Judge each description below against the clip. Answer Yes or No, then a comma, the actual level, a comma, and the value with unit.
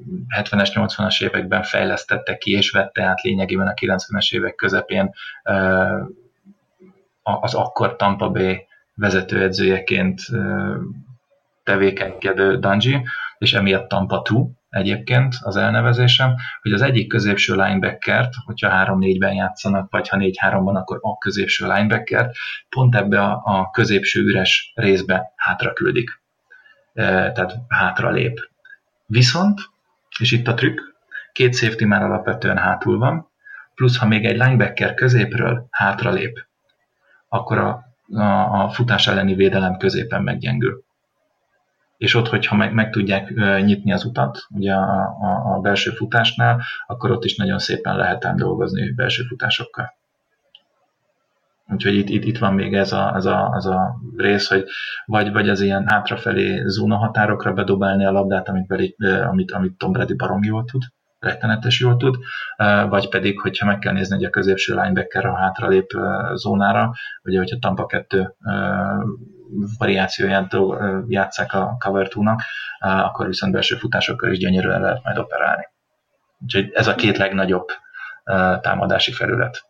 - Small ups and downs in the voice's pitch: No, average, 3.4 semitones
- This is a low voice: Yes, low, 100 Hz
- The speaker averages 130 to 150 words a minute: Yes, average, 135 wpm